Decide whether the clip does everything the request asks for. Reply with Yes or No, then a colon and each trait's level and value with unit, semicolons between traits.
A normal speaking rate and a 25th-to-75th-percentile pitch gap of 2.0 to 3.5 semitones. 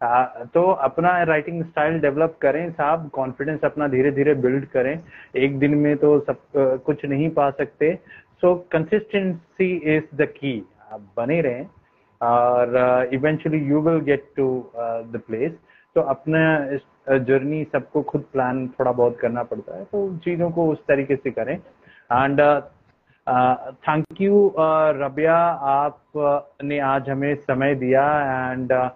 Yes: average, 140 wpm; average, 3.0 semitones